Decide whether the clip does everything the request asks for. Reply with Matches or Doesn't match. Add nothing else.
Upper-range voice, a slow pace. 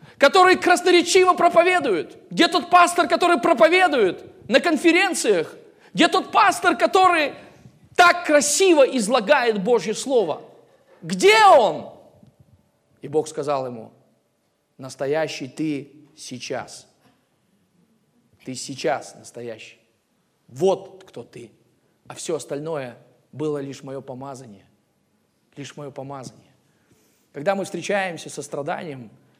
Matches